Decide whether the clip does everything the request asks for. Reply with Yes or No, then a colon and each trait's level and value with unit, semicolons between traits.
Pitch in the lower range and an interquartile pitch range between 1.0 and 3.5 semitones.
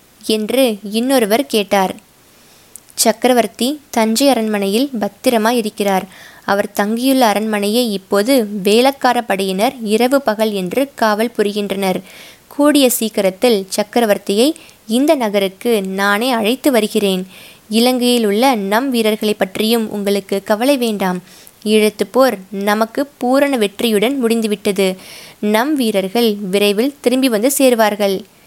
No: high, 220 Hz; average, 3.2 semitones